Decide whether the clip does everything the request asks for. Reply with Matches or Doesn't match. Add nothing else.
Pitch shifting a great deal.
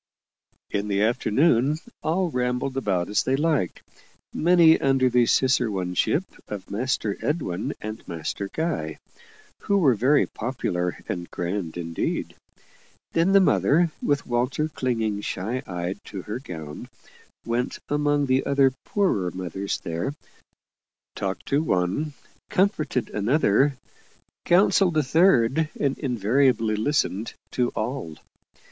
Matches